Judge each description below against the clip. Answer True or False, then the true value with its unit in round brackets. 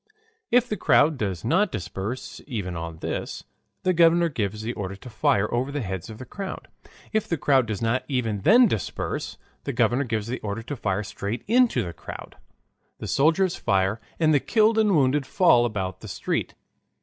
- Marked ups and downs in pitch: True (8.2 semitones)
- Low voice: True (120 Hz)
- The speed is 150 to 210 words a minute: True (185 wpm)